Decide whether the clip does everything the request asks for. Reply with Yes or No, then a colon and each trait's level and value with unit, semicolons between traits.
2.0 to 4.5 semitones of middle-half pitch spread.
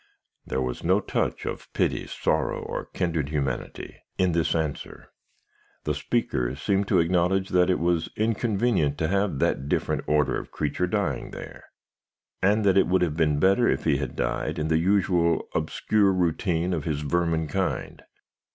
Yes: average, 4.2 semitones